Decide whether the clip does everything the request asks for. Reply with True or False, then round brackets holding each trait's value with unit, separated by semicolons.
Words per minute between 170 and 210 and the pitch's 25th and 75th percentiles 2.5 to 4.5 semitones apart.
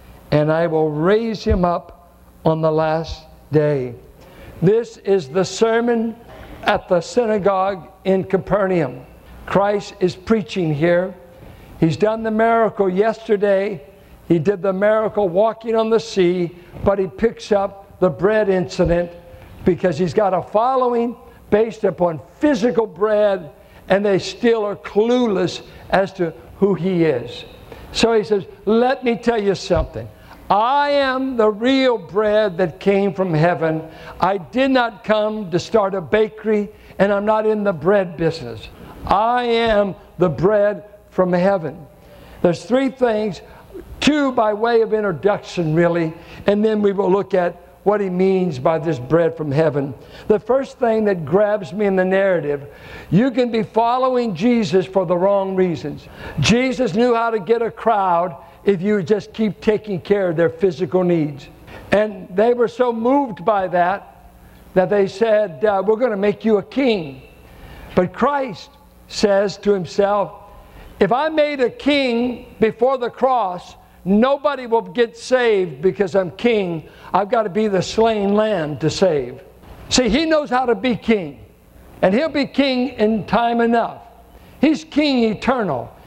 False (155 wpm; 4.0 semitones)